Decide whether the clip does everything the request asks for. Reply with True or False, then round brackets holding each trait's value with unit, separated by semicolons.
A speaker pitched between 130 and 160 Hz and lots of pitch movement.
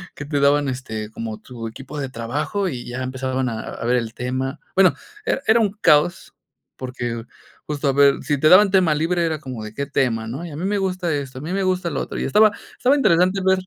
True (140 Hz; 6.0 semitones)